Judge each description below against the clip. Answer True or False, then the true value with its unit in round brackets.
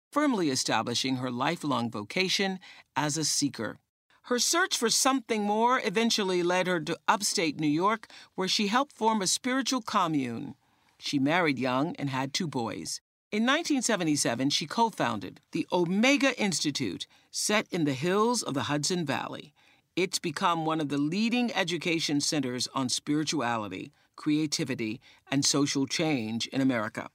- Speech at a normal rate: True (145 wpm)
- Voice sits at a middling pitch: True (170 Hz)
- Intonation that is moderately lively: False (7.6 semitones)